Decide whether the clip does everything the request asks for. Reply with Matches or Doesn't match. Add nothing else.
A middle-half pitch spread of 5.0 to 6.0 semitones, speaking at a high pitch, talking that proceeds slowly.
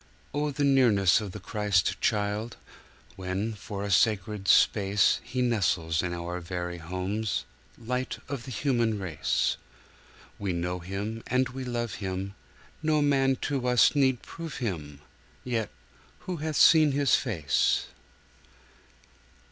Doesn't match